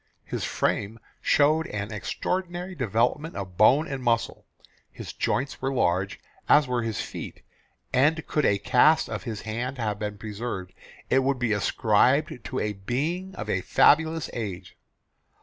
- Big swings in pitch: Yes, wide, 5.9 semitones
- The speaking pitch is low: Yes, low, 125 Hz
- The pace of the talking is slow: No, average, 150 wpm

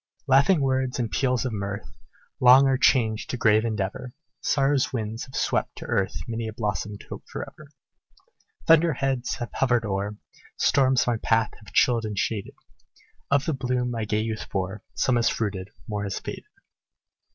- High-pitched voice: No, low, 115 Hz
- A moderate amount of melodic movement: Yes, average, 3.7 semitones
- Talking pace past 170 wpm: No, average, 165 wpm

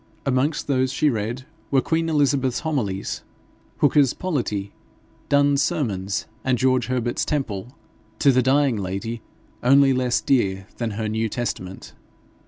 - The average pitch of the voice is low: Yes, low, 130 Hz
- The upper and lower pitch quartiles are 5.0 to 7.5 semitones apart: No, average, 4.2 semitones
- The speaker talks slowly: Yes, slow, 130 wpm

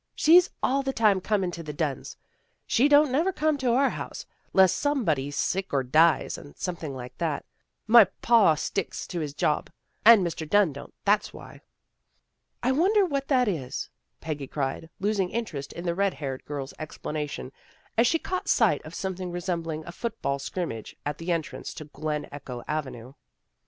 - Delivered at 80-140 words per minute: No, average, 185 wpm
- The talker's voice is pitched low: No, medium, 175 Hz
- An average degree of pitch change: No, wide, 7.7 semitones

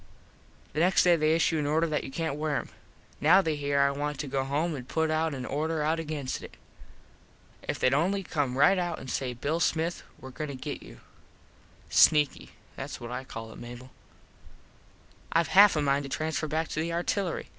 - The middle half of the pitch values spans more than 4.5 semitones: No, average, 2.8 semitones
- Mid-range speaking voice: Yes, medium, 150 Hz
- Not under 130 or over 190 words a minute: No, average, 200 wpm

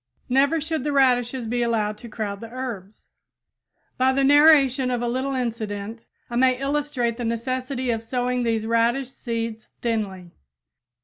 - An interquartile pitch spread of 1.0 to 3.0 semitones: Yes, narrow, 2.6 semitones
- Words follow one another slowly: No, average, 150 wpm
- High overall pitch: Yes, high, 245 Hz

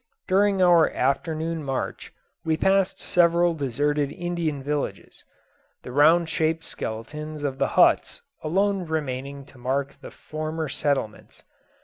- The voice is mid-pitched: Yes, medium, 155 Hz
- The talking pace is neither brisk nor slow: No, slow, 120 wpm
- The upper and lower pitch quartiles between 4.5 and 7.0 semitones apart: No, average, 3.4 semitones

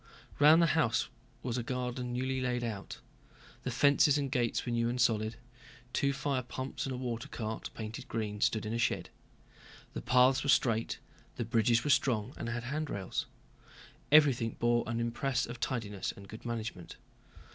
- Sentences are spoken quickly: No, average, 170 wpm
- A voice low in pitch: Yes, low, 120 Hz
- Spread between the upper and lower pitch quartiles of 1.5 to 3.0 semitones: Yes, narrow, 2.5 semitones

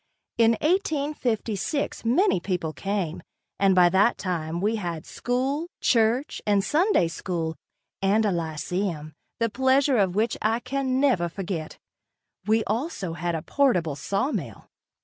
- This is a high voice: Yes, high, 210 Hz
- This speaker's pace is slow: Yes, slow, 130 wpm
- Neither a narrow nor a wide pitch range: No, wide, 6.7 semitones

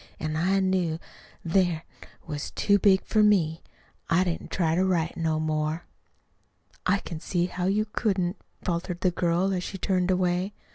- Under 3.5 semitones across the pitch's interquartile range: Yes, narrow, 2.4 semitones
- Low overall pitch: No, medium, 180 Hz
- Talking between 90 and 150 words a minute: No, average, 160 wpm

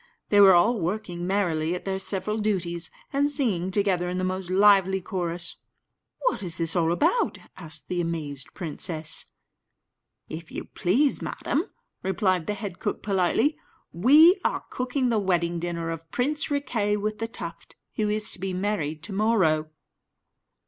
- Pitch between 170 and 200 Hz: Yes, high, 190 Hz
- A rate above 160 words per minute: No, average, 155 wpm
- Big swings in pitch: No, average, 3.8 semitones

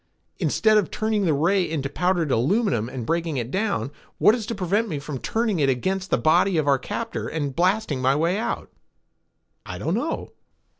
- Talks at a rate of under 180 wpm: No, average, 190 wpm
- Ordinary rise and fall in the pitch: No, wide, 6.4 semitones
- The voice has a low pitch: No, medium, 170 Hz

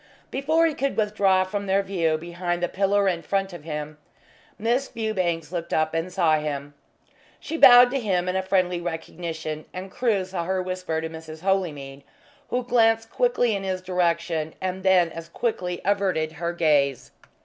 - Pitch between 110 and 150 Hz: No, medium, 185 Hz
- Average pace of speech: Yes, average, 170 wpm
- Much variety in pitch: No, average, 3.6 semitones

